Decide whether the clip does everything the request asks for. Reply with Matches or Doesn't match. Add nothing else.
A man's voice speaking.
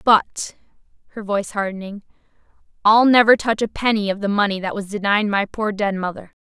Doesn't match